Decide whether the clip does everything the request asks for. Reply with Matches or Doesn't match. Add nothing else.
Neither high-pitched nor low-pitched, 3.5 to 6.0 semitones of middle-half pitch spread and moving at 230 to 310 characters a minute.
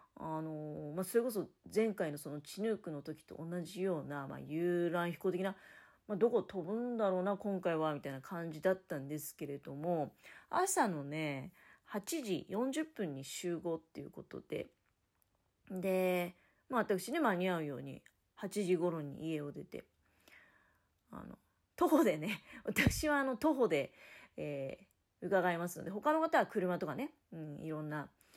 Matches